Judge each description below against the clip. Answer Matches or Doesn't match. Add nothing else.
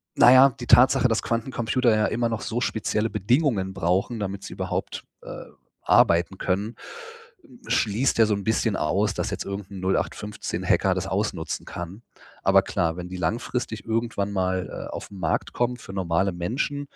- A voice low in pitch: Matches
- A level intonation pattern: Doesn't match